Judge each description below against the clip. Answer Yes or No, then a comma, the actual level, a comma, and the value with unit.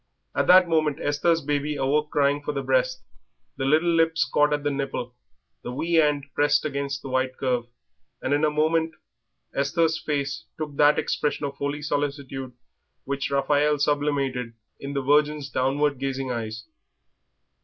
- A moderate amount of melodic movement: No, narrow, 1.6 semitones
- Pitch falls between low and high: Yes, medium, 145 Hz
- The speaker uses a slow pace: No, average, 155 wpm